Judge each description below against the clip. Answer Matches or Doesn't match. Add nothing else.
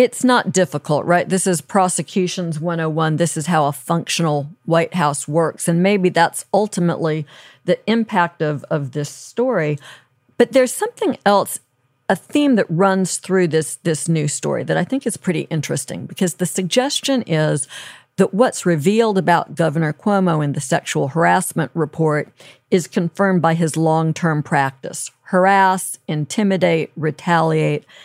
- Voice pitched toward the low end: Doesn't match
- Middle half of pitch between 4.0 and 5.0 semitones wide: Doesn't match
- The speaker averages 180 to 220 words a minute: Doesn't match